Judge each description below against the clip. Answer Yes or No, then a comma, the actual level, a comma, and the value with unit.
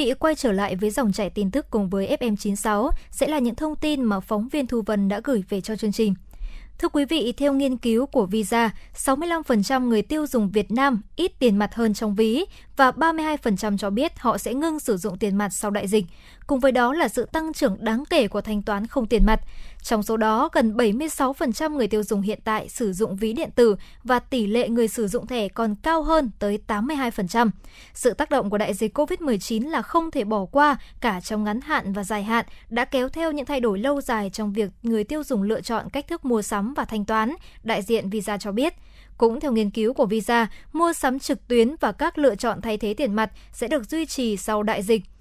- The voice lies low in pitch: No, high, 230 Hz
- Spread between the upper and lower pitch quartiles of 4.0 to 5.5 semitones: Yes, average, 4.5 semitones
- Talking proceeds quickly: No, average, 230 wpm